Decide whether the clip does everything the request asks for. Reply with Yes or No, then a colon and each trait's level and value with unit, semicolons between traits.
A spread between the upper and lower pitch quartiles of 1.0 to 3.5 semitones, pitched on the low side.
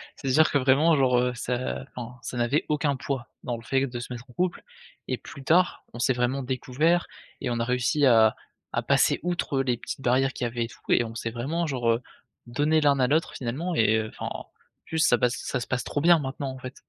Yes: average, 3.1 semitones; low, 130 Hz